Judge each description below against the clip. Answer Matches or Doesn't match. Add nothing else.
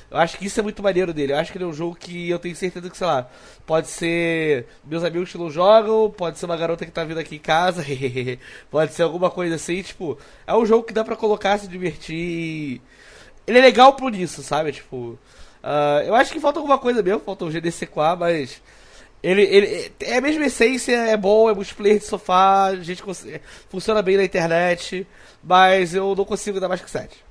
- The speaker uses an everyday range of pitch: Matches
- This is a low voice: Doesn't match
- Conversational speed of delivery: Doesn't match